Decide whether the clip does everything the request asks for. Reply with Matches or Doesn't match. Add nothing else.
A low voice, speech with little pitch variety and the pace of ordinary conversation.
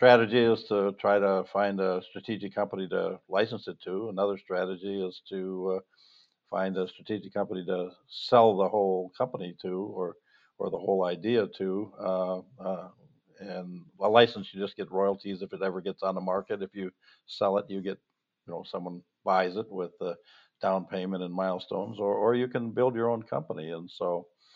Matches